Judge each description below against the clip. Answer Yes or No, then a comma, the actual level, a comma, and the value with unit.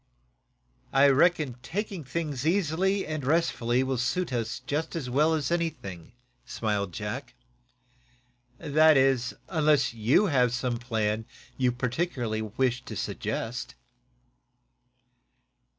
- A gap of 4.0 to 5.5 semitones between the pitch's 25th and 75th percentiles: Yes, average, 4.9 semitones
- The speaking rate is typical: No, slow, 105 wpm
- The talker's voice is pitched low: Yes, low, 130 Hz